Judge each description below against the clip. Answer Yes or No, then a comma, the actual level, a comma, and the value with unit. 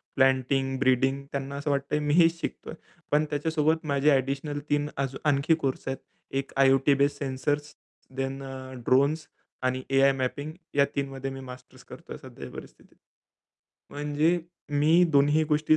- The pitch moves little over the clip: Yes, narrow, 1.7 semitones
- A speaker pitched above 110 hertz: Yes, medium, 140 Hz